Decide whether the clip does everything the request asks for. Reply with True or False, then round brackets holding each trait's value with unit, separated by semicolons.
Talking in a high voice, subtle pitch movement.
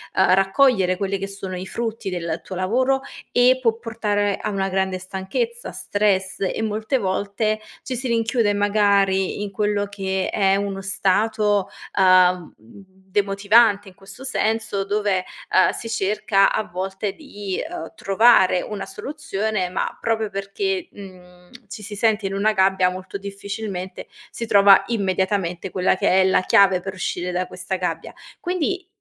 True (200 Hz; 2.3 semitones)